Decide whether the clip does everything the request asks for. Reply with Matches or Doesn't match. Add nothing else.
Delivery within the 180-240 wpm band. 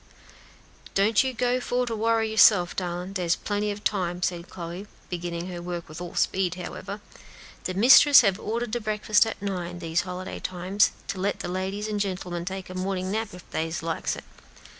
Matches